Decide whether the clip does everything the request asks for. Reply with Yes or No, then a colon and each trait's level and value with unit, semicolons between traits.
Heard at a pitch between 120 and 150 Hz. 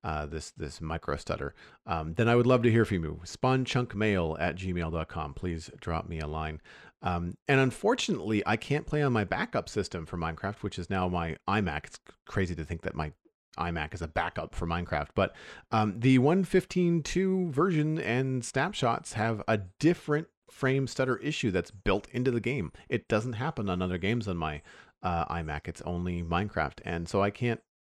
No: low, 100 Hz